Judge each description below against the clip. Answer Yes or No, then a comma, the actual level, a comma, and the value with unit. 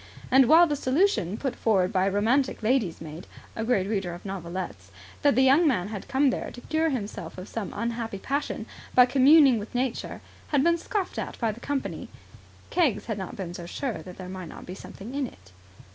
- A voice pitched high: Yes, high, 230 Hz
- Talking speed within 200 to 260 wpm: Yes, fast, 205 wpm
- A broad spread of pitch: Yes, wide, 6.3 semitones